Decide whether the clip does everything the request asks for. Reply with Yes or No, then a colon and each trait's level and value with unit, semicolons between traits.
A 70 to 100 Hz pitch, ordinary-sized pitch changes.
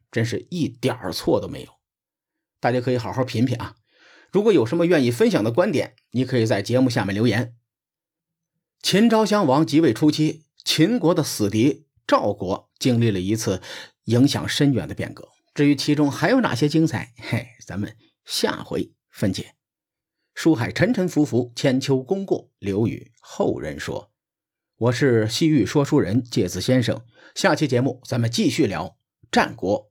No: low, 130 Hz; average, 4.8 semitones